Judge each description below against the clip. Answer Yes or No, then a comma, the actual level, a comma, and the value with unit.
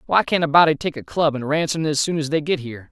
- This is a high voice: No, medium, 150 Hz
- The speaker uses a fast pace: Yes, fast, 330 wpm